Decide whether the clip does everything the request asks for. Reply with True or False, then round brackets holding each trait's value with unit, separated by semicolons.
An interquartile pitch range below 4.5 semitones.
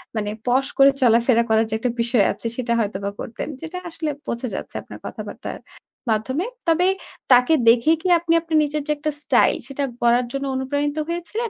False (4.9 semitones)